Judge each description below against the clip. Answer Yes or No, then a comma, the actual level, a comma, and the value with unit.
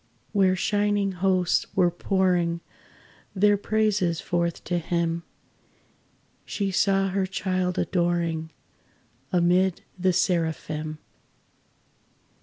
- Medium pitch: Yes, medium, 180 Hz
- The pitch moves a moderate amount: No, narrow, 2.2 semitones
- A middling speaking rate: No, slow, 85 wpm